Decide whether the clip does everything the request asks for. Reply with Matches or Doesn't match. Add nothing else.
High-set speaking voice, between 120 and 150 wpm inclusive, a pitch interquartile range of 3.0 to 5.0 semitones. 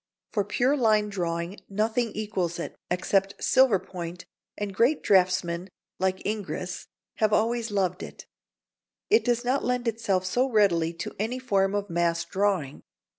Matches